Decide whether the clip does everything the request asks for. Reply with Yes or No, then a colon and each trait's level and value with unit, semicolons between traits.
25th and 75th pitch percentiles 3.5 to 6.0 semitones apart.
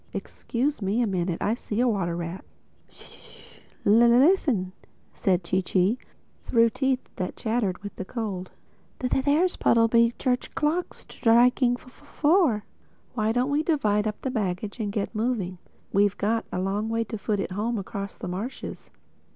Yes: average, 4.1 semitones